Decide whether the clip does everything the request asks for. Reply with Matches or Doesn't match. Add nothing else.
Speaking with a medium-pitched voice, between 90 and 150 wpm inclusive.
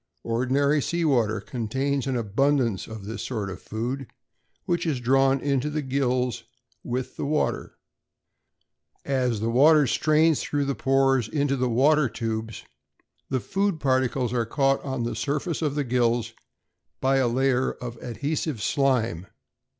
Doesn't match